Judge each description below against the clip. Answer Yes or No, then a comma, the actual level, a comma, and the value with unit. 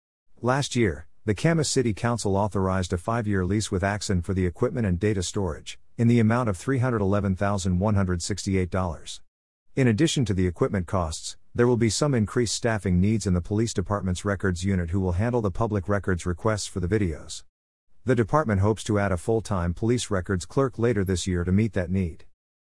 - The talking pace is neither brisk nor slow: Yes, average, 185 wpm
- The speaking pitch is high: No, low, 100 Hz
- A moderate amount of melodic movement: Yes, average, 3.7 semitones